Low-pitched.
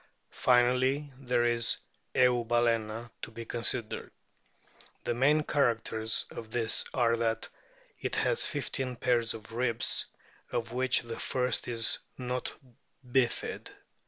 Yes: low, 120 Hz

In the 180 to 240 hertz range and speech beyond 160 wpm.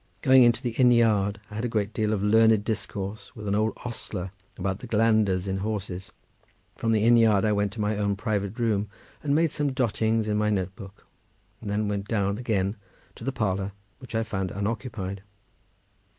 No: low, 105 Hz; average, 195 wpm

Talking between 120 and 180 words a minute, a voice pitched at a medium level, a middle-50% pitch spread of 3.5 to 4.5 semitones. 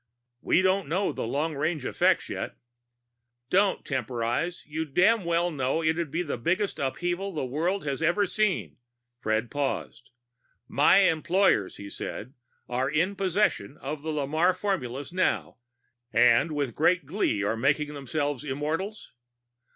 No: average, 145 wpm; medium, 155 Hz; average, 5.2 semitones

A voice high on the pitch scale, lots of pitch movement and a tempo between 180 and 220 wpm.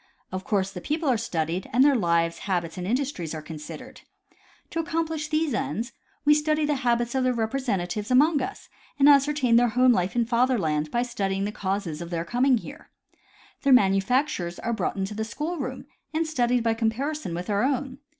Yes: high, 235 Hz; wide, 6.4 semitones; average, 200 wpm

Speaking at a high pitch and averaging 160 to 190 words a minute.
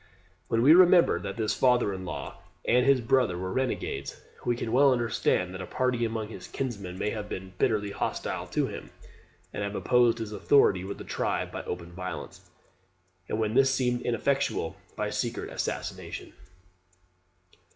No: low, 115 Hz; average, 170 wpm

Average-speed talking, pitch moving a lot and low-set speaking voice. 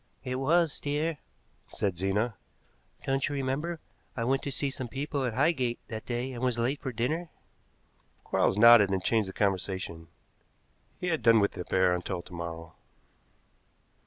Yes: average, 160 wpm; wide, 6.1 semitones; low, 120 Hz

